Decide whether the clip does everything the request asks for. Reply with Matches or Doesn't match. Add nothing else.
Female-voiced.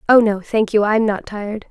Matches